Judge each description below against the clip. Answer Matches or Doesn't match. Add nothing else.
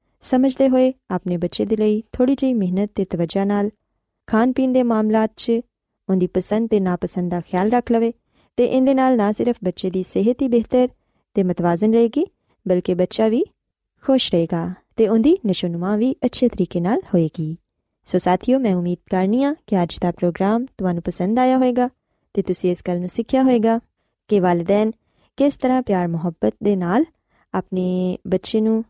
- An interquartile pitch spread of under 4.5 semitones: Doesn't match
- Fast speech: Matches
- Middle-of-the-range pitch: Doesn't match